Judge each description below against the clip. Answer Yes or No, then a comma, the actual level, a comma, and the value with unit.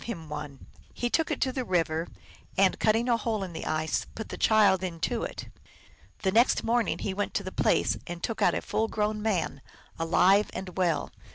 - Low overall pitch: No, high, 195 Hz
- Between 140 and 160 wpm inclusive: No, average, 200 wpm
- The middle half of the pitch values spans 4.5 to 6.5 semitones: Yes, average, 4.9 semitones